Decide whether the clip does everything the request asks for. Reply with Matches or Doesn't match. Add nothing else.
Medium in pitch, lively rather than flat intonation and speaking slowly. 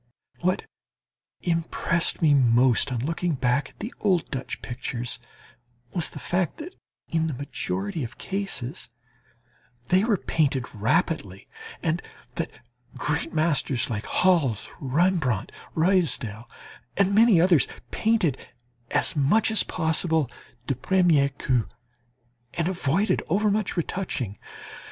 Matches